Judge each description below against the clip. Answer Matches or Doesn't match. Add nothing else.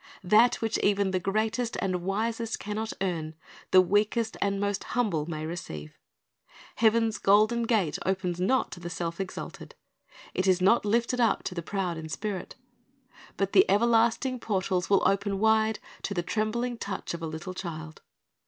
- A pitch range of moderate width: Matches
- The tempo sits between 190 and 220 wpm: Doesn't match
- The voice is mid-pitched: Doesn't match